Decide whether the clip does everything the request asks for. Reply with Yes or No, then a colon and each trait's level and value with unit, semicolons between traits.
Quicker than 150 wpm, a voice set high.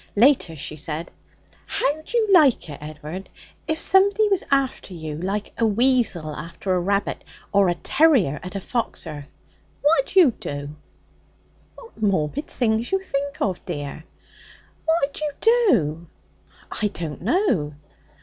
No: average, 140 wpm; high, 205 Hz